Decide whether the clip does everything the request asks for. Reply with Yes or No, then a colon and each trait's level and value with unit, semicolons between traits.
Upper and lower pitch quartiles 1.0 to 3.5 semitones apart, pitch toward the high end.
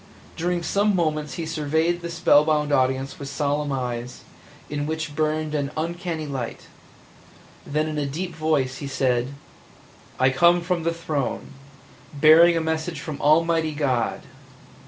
No: average, 2.9 semitones; medium, 155 Hz